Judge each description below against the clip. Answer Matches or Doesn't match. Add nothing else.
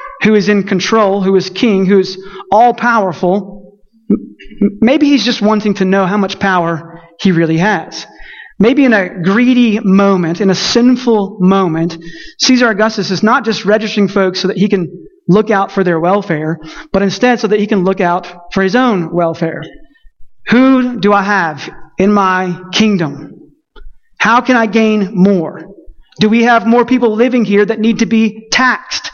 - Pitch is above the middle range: Matches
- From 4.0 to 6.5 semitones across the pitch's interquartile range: Doesn't match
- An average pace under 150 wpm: Doesn't match